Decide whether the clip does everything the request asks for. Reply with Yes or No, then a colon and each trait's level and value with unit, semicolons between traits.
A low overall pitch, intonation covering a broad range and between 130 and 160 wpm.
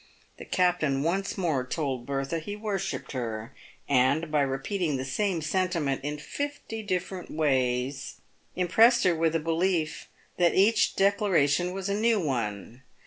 No: medium, 165 Hz; wide, 5.8 semitones; average, 145 wpm